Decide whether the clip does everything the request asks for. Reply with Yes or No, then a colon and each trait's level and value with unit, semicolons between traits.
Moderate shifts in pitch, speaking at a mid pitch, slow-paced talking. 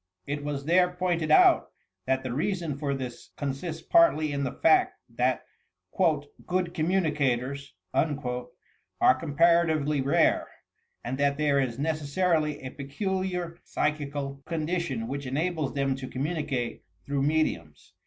Yes: average, 3.6 semitones; medium, 150 Hz; slow, 125 wpm